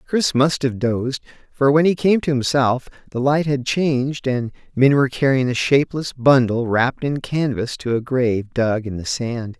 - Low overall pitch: Yes, low, 130 Hz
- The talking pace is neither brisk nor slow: Yes, average, 195 wpm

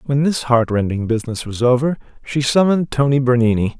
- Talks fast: No, average, 160 wpm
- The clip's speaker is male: Yes, male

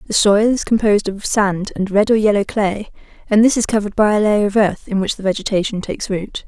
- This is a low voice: No, high, 205 Hz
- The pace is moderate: No, fast, 240 wpm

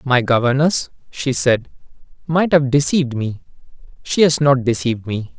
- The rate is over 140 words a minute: No, slow, 135 wpm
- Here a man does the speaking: Yes, male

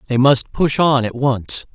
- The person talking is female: No, male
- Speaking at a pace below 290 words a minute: Yes, fast, 205 wpm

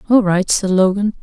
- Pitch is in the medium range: No, high, 200 Hz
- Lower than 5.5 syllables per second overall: Yes, 5.1 syllables/s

